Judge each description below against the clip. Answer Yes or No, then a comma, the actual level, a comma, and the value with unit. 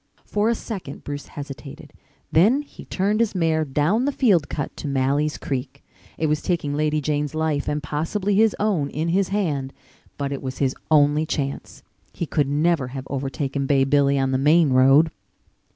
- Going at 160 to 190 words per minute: Yes, average, 180 wpm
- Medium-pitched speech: Yes, medium, 150 Hz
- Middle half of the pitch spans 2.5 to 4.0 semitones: Yes, average, 3.5 semitones